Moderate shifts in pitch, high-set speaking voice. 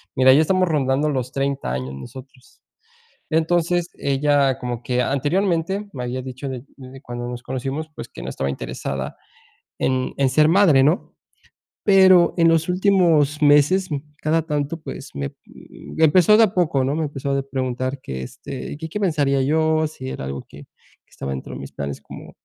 No: average, 4.0 semitones; medium, 140 Hz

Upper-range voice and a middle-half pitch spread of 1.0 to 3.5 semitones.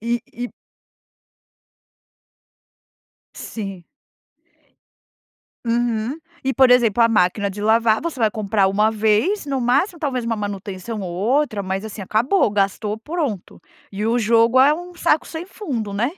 No: high, 225 Hz; average, 4.0 semitones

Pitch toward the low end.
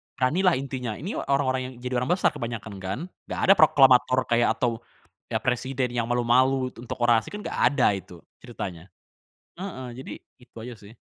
Yes: low, 125 Hz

